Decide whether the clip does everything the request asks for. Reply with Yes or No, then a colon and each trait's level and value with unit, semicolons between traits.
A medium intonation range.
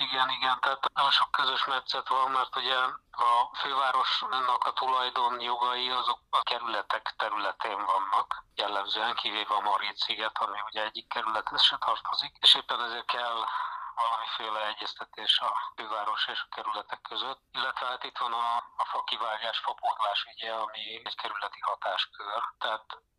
No: narrow, 1.5 semitones